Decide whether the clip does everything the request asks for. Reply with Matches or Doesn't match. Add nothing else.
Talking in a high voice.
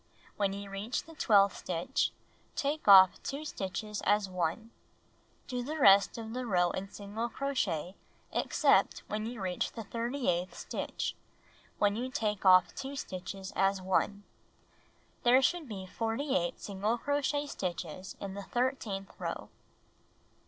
Matches